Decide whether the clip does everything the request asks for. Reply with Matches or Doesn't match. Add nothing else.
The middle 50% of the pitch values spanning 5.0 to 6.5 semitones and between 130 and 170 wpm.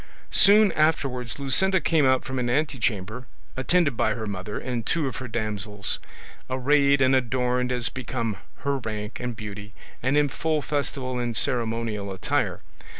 Doesn't match